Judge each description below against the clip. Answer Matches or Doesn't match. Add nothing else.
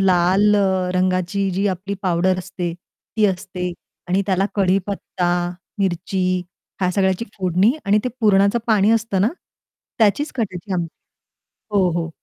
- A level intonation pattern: Matches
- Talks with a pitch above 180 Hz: Matches